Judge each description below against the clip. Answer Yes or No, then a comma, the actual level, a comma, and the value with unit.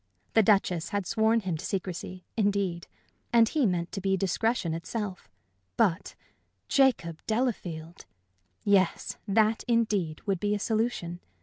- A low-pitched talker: No, high, 200 Hz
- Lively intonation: No, average, 4.2 semitones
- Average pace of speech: No, slow, 130 wpm